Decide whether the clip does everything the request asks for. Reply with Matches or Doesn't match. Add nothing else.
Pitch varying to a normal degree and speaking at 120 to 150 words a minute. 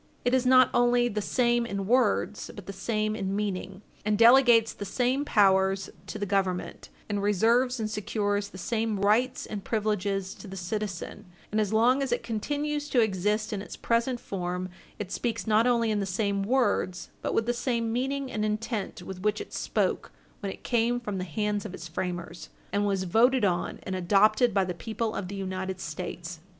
Doesn't match